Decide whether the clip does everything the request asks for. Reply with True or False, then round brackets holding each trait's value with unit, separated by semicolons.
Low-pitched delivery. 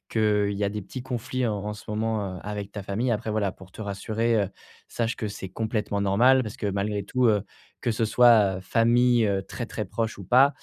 True (105 Hz)